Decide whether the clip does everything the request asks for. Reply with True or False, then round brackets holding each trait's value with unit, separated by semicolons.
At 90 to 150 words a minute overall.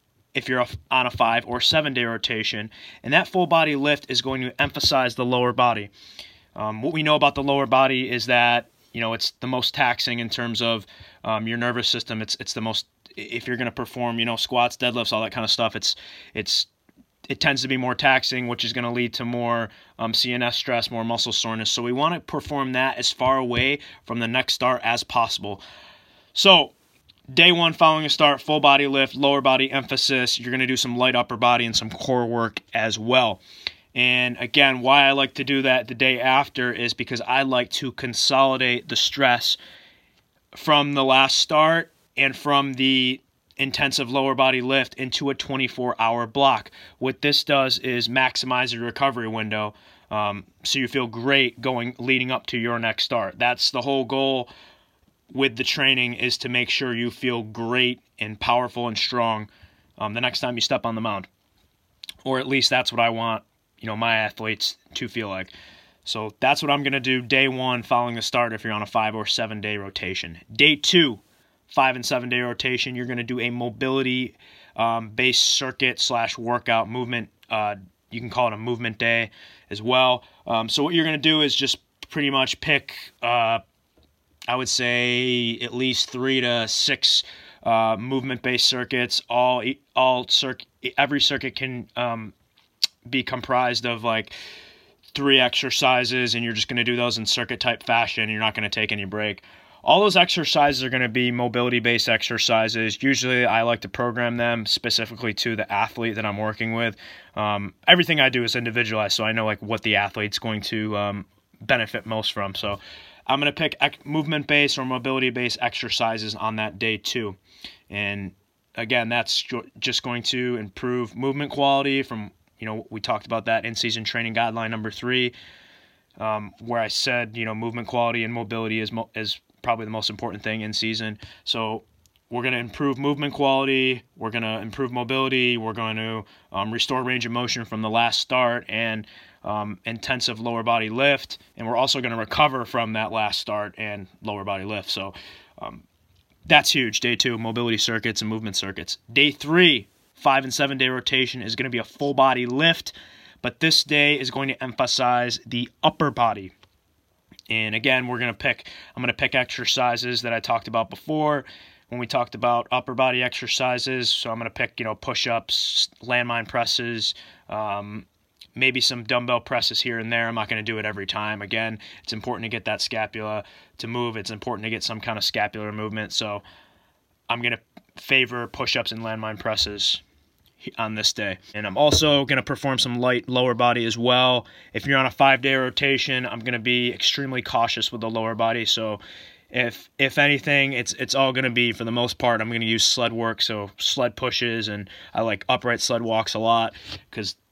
False (195 wpm)